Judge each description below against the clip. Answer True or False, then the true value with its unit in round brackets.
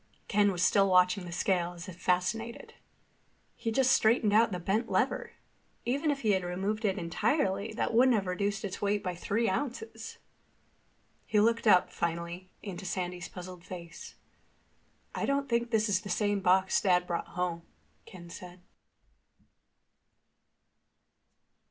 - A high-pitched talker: True (195 Hz)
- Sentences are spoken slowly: False (145 wpm)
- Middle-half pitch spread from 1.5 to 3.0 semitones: False (3.5 semitones)